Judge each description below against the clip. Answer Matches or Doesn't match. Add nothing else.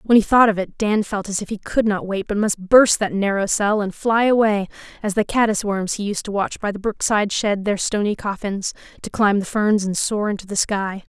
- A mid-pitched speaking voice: Doesn't match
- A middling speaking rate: Doesn't match